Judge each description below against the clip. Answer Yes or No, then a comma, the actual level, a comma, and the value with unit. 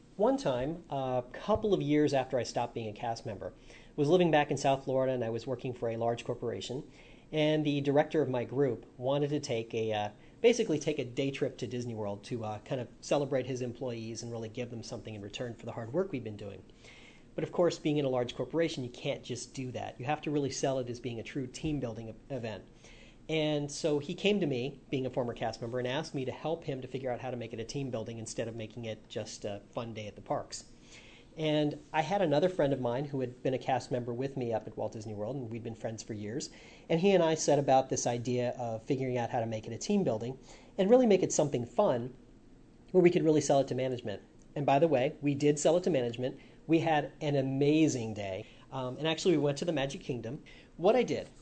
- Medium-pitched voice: No, low, 130 Hz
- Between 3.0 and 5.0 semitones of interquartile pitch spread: Yes, average, 4.1 semitones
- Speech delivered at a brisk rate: Yes, fast, 255 wpm